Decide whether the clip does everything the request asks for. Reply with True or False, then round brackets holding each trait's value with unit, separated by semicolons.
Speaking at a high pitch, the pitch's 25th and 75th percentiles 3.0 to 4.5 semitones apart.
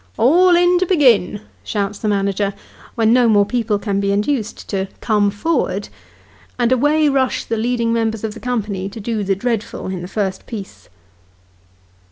True (220 Hz; 3.7 semitones)